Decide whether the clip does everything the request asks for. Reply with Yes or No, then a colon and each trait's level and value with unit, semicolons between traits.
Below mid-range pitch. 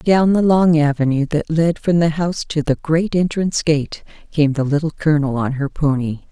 No: medium, 155 Hz